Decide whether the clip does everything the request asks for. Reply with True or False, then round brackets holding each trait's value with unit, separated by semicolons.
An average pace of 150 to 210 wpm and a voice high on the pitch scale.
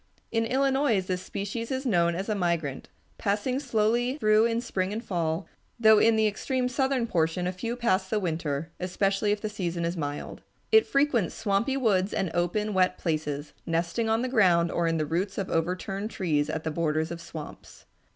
True (190 wpm; 195 Hz)